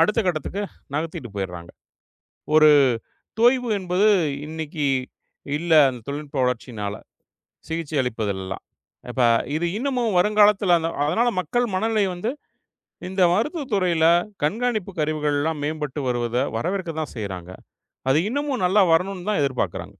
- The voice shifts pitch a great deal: Yes, wide, 6.9 semitones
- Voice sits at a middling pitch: Yes, medium, 160 Hz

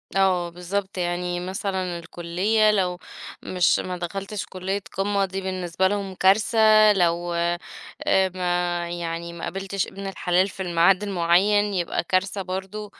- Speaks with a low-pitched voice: No, medium, 185 Hz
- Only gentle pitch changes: Yes, narrow, 2.1 semitones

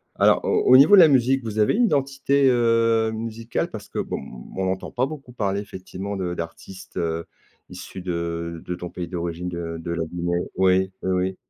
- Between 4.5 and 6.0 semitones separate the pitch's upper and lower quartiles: Yes, average, 5.3 semitones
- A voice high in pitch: No, very low, 95 Hz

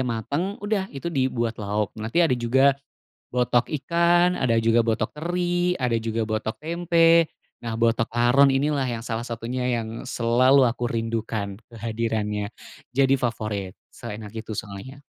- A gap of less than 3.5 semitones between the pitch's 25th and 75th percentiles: No, average, 3.8 semitones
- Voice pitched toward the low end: Yes, low, 120 Hz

